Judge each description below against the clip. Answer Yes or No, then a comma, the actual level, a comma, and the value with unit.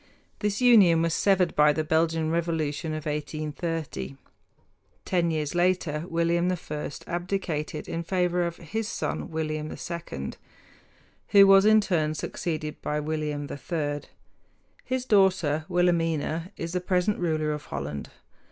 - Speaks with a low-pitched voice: No, medium, 165 Hz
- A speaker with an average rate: No, slow, 130 wpm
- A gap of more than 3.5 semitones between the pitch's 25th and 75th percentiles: No, average, 2.9 semitones